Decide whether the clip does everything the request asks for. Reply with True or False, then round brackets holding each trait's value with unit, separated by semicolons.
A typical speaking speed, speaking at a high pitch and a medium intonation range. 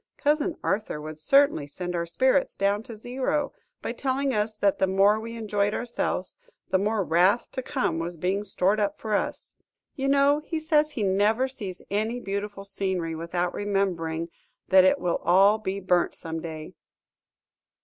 True (170 wpm; 200 Hz; 5.0 semitones)